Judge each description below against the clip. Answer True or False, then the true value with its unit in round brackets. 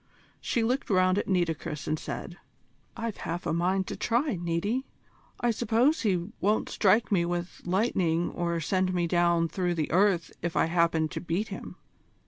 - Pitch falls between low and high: True (180 Hz)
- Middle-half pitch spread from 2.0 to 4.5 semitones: True (3.6 semitones)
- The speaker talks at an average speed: True (170 wpm)